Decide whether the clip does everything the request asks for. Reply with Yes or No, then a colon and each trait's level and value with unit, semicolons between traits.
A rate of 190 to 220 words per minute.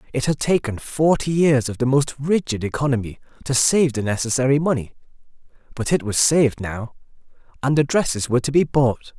No: average, 175 wpm